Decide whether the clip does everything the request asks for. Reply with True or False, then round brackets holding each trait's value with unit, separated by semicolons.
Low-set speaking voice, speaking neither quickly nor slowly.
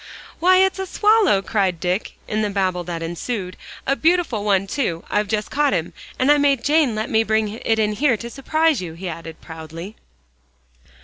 False (215 Hz; 190 wpm)